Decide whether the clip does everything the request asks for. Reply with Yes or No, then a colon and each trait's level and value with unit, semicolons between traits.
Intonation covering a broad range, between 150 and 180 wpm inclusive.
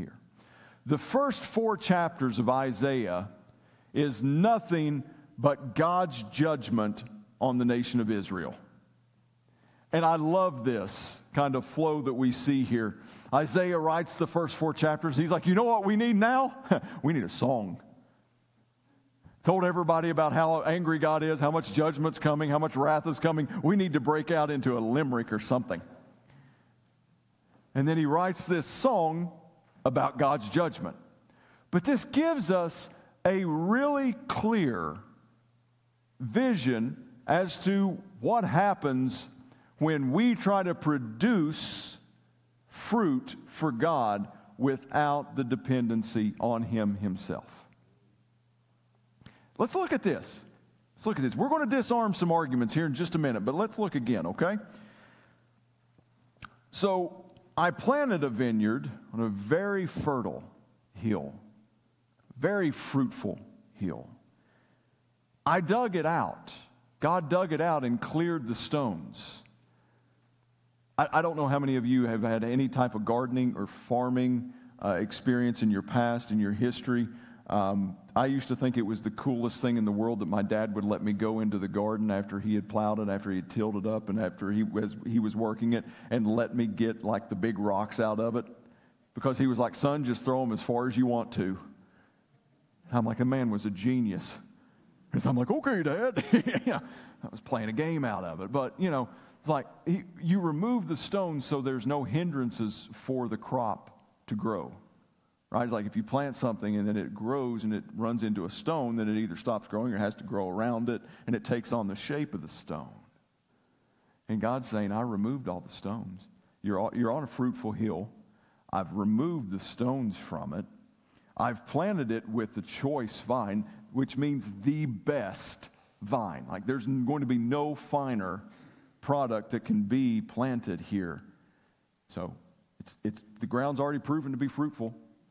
Yes: wide, 6.1 semitones; average, 170 wpm